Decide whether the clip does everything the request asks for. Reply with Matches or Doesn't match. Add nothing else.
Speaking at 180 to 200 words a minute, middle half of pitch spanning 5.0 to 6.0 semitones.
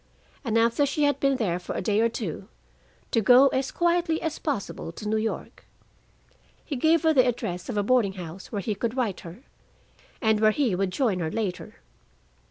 Matches